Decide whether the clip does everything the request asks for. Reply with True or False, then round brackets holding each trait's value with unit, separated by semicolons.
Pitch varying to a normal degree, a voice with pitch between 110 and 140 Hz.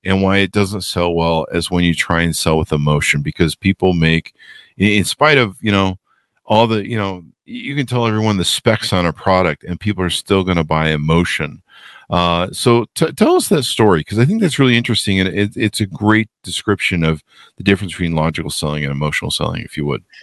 False (4.5 semitones; 95 Hz)